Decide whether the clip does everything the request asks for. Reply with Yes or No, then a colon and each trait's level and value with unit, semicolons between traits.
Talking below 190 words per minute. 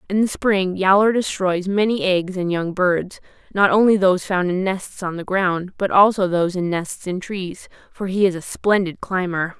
No: average, 200 wpm